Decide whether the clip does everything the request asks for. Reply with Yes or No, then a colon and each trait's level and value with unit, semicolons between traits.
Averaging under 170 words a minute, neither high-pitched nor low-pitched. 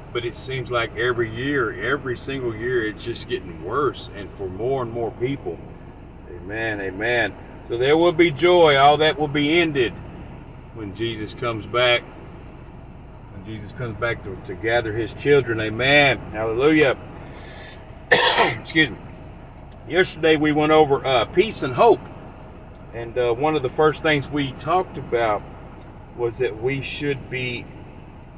No: average, 150 wpm; low, 125 Hz